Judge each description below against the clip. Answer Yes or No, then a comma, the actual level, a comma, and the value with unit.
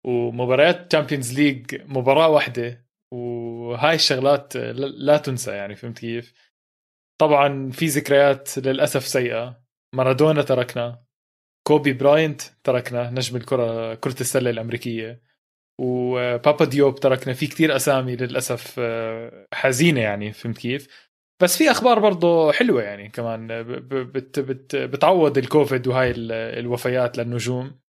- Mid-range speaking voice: No, low, 130 Hz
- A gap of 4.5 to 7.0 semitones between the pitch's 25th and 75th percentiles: No, average, 2.9 semitones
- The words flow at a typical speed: Yes, average, 110 wpm